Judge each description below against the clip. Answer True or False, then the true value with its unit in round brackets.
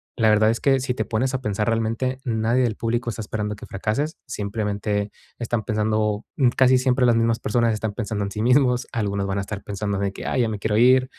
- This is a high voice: False (110 Hz)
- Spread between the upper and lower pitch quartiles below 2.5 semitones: False (2.9 semitones)